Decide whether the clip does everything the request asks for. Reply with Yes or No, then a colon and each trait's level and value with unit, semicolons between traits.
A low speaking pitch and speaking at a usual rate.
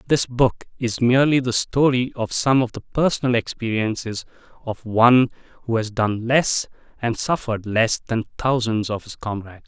Yes: low, 120 Hz; average, 160 wpm